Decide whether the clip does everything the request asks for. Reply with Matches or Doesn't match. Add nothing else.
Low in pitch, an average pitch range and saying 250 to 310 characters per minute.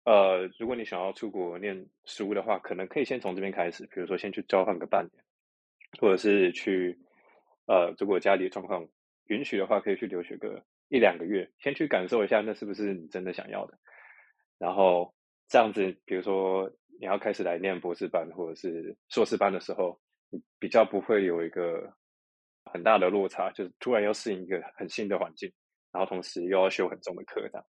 Doesn't match